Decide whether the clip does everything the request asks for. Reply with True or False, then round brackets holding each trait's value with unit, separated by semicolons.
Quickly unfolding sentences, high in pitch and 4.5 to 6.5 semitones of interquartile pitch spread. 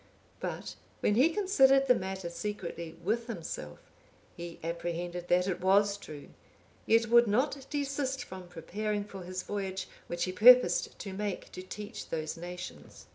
False (150 wpm; 195 Hz; 5.1 semitones)